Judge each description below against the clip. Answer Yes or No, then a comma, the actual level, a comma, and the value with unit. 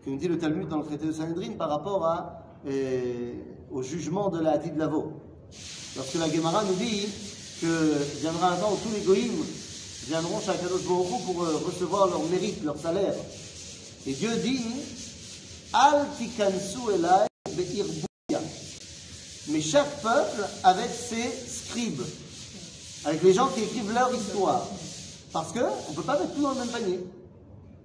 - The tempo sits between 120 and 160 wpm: Yes, average, 150 wpm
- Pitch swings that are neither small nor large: No, wide, 6.3 semitones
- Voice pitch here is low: No, medium, 185 Hz